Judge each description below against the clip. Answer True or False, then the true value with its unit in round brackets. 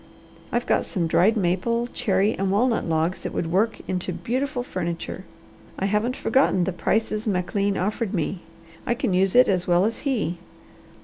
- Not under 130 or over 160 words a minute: False (170 wpm)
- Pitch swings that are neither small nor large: True (4.0 semitones)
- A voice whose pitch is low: False (195 Hz)